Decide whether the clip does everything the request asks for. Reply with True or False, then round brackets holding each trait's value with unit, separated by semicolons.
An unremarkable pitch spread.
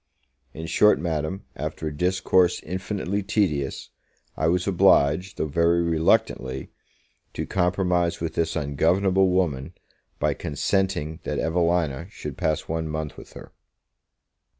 True (3.1 semitones)